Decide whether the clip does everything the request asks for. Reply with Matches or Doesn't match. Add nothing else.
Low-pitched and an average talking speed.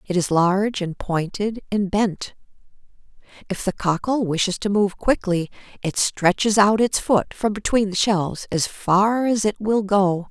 Doesn't match